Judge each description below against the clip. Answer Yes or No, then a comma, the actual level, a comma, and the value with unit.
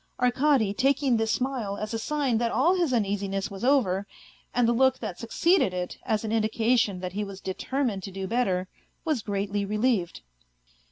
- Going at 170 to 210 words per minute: Yes, average, 180 wpm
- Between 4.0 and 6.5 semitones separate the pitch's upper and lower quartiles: Yes, average, 4.5 semitones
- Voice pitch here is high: Yes, high, 225 Hz